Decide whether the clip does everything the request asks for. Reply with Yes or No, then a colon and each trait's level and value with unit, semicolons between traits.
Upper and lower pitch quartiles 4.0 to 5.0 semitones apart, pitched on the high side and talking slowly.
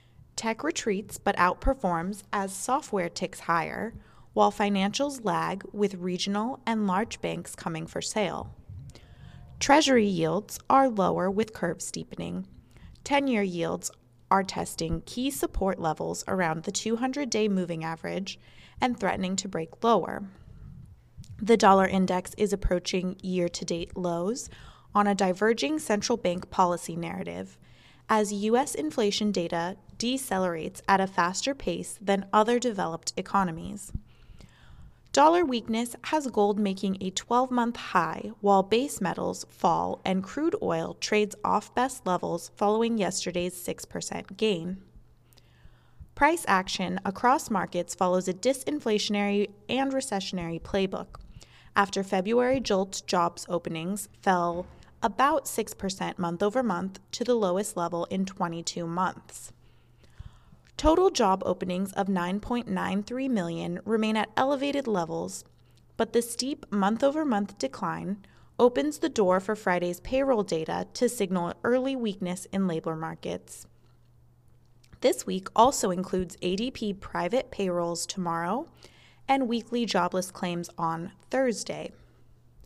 Yes: average, 4.5 semitones; high, 195 Hz; slow, 120 wpm